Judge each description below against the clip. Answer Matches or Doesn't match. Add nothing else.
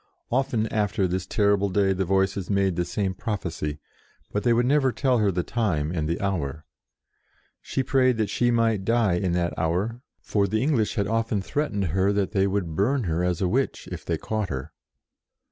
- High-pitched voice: Doesn't match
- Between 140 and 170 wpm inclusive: Doesn't match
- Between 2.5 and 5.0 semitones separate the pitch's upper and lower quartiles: Matches